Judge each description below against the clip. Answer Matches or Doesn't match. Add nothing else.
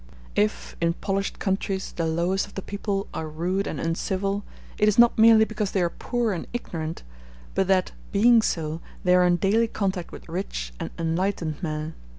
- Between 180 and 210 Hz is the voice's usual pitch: Matches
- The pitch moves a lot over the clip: Doesn't match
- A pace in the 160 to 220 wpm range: Matches